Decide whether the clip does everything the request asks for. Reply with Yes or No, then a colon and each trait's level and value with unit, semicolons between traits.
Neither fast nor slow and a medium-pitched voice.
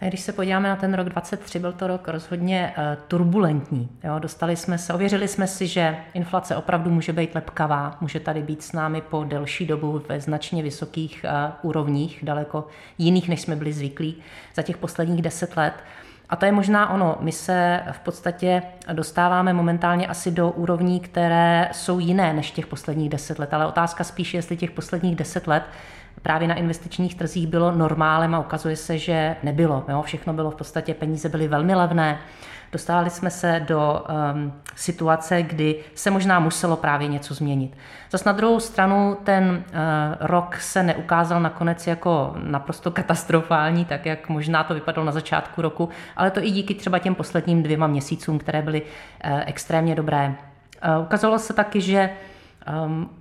No: fast, 175 wpm; medium, 165 Hz